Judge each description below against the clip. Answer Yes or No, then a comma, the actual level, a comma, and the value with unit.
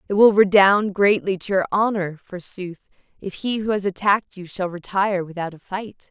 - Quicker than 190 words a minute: No, average, 185 wpm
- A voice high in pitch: Yes, high, 195 Hz